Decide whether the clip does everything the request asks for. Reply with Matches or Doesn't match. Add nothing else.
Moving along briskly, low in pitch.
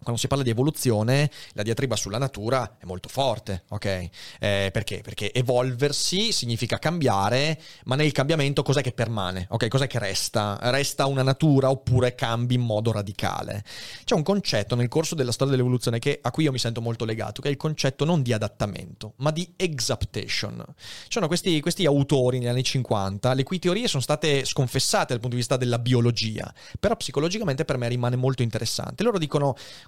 Matches